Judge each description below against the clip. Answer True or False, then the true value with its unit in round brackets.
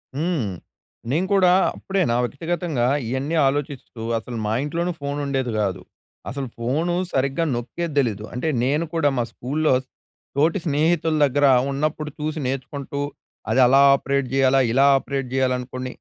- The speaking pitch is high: False (140 Hz)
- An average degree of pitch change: True (3.5 semitones)